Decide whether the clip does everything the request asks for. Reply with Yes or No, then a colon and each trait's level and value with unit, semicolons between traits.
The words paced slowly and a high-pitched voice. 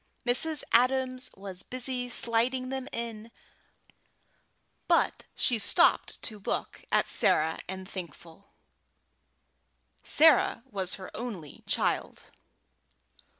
Yes: slow, 95 wpm; high, 230 Hz